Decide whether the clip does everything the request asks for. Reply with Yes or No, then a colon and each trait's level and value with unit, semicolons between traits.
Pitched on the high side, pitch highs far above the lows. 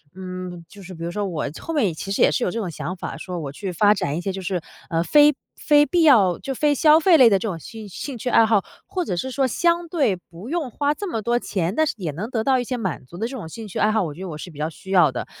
Yes: high, 205 Hz; wide, 7.0 semitones